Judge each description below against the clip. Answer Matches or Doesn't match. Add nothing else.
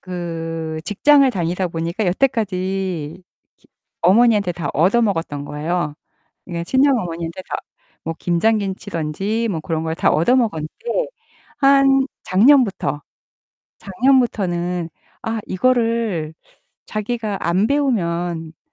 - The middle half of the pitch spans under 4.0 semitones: Doesn't match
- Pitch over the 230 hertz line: Doesn't match